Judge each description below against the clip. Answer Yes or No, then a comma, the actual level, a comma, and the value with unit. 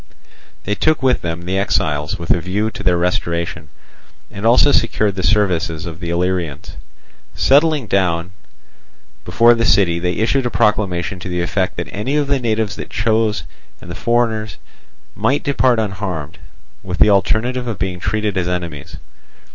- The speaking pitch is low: Yes, low, 100 Hz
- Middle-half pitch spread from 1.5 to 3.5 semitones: No, average, 4.4 semitones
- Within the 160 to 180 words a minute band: Yes, average, 165 wpm